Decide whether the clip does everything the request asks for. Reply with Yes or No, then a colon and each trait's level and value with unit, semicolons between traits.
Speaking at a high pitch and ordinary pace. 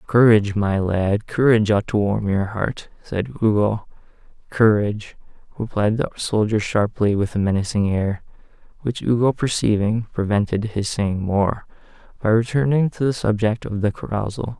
No: low, 110 Hz; average, 145 wpm